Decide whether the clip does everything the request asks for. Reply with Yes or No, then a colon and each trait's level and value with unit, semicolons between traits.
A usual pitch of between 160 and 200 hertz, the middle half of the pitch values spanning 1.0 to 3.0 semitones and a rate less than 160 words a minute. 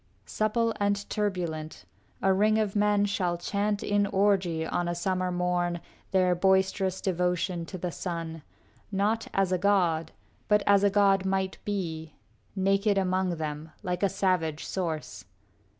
Yes: high, 190 Hz; average, 2.7 semitones; average, 150 wpm